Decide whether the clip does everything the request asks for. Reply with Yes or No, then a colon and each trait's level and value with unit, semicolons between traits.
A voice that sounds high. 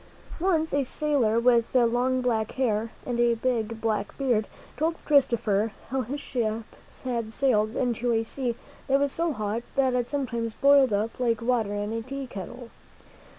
Yes: high, 240 Hz